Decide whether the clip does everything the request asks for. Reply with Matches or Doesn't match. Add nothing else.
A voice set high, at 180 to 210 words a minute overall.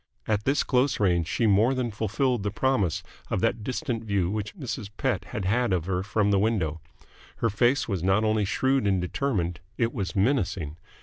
Doesn't match